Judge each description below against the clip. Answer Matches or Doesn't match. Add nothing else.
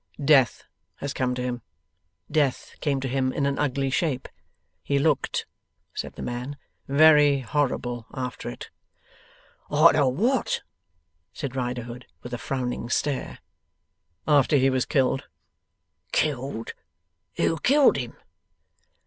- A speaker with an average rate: Doesn't match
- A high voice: Doesn't match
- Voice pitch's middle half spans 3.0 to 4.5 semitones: Doesn't match